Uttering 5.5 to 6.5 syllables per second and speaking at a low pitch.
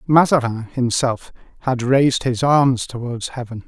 No: 4.5 syllables/s; low, 125 Hz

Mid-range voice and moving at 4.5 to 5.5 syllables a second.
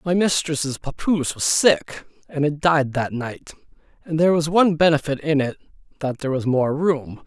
Yes: medium, 150 Hz; 5.0 syllables/s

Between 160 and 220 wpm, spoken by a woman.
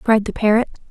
Yes: average, 200 wpm; female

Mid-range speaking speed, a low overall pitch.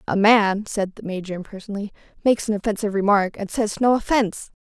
No: average, 180 wpm; high, 210 Hz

